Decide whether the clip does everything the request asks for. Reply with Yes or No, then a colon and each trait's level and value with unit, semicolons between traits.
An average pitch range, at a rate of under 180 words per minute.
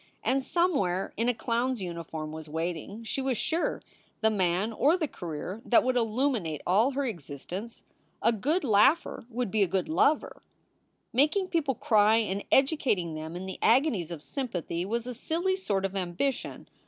No: wide, 6.9 semitones; average, 170 wpm